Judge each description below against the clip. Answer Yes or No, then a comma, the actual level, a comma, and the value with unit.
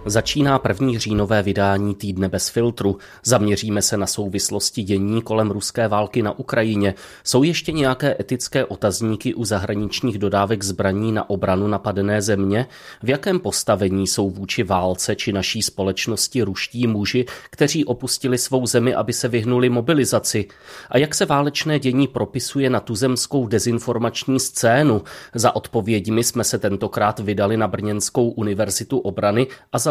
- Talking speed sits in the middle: Yes, average, 140 wpm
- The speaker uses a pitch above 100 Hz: Yes, low, 115 Hz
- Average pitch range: Yes, average, 3.6 semitones